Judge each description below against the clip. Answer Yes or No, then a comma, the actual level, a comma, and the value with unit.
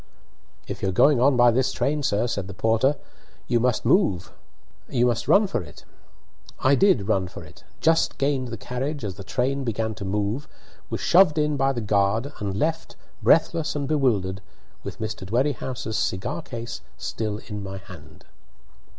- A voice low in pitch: Yes, low, 120 Hz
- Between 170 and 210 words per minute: No, average, 160 wpm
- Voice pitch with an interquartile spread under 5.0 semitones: No, wide, 5.6 semitones